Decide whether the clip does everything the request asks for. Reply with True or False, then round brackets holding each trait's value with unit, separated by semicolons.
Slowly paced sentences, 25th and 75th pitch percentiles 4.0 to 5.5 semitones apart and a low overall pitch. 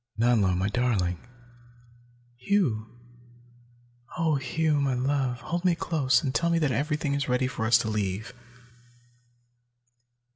True (125 wpm; 5.1 semitones; 130 Hz)